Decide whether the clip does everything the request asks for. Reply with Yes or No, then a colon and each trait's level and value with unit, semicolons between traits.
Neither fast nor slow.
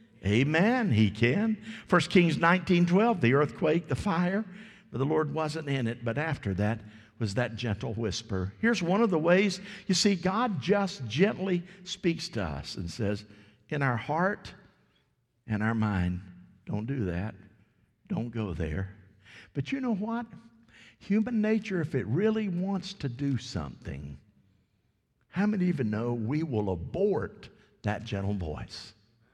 Yes: average, 150 wpm